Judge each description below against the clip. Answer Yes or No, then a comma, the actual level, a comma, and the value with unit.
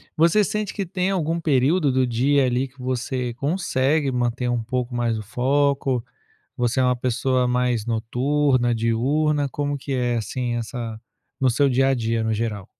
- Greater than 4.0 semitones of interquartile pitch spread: No, average, 3.0 semitones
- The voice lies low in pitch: Yes, low, 130 Hz